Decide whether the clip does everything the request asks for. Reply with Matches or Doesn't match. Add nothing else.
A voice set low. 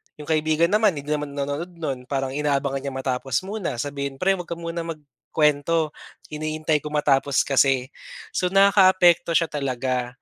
Doesn't match